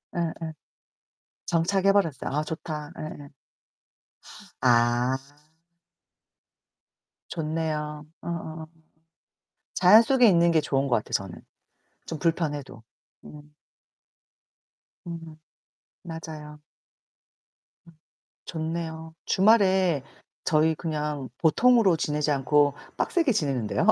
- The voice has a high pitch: No, medium, 160 Hz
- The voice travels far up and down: No, narrow, 2.5 semitones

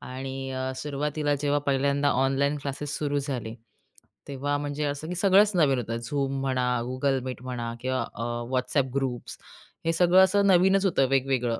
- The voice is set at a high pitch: No, medium, 140 Hz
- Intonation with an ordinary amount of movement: No, narrow, 2.2 semitones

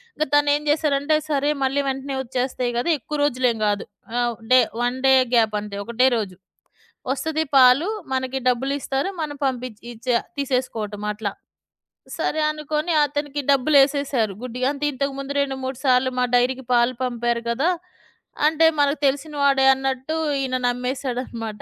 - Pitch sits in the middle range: No, very high, 265 Hz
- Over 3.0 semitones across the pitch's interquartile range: No, average, 2.7 semitones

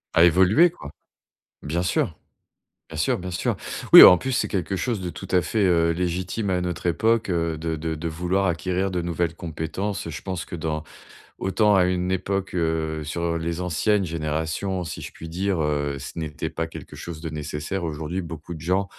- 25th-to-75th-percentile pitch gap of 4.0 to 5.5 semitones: No, narrow, 2.6 semitones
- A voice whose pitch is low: Yes, very low, 85 Hz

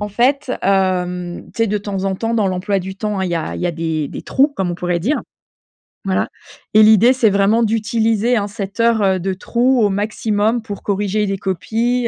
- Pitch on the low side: No, high, 205 Hz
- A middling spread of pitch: Yes, average, 3.1 semitones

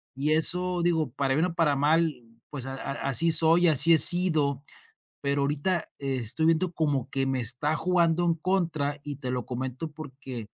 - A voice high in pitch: No, medium, 150 Hz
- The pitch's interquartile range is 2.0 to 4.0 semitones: Yes, average, 3.6 semitones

